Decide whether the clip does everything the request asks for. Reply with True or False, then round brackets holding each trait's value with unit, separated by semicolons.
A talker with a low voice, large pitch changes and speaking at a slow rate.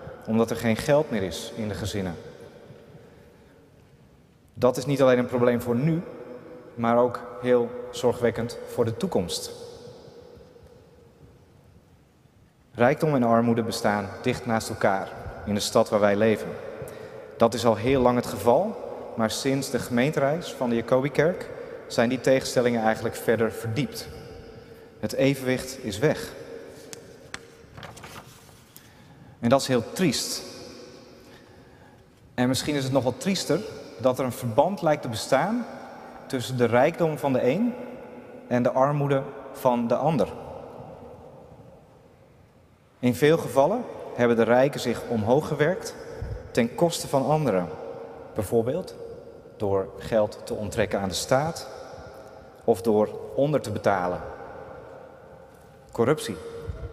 True (130 Hz; 6.0 semitones; 125 wpm)